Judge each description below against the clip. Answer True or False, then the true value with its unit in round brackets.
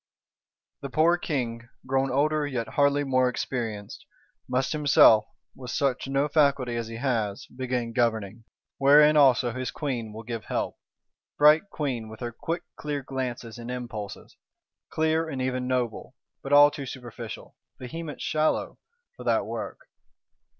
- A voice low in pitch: True (130 Hz)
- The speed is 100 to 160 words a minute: True (145 wpm)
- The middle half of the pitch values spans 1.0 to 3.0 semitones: False (3.5 semitones)